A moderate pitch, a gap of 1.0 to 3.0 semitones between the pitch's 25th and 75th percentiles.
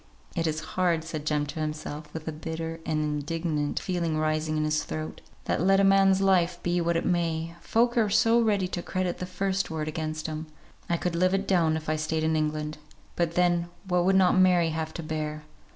Yes: medium, 165 Hz; average, 2.7 semitones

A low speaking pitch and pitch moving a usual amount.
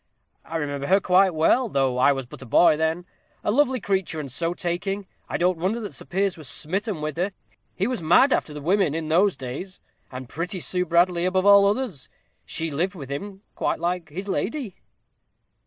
No: medium, 180 Hz; average, 4.1 semitones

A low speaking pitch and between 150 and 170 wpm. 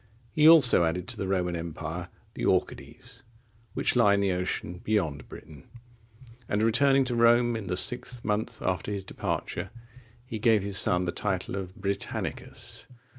Yes: low, 100 Hz; average, 160 wpm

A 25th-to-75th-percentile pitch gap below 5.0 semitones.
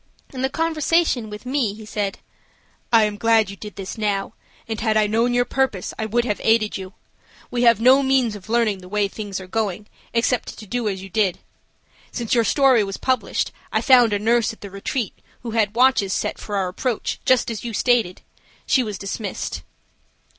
Yes: average, 3.1 semitones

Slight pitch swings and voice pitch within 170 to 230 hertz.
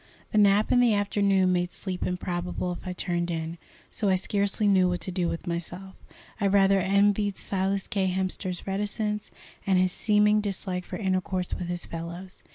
Yes: narrow, 2.0 semitones; high, 190 Hz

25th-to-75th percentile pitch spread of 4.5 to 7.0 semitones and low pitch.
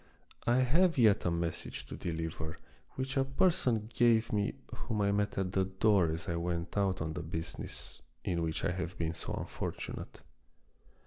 Yes: average, 5.3 semitones; very low, 95 Hz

